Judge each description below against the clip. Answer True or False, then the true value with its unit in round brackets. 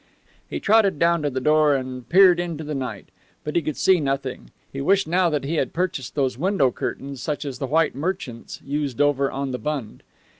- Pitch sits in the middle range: True (145 Hz)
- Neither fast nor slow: False (210 wpm)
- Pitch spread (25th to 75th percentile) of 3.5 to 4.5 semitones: True (3.9 semitones)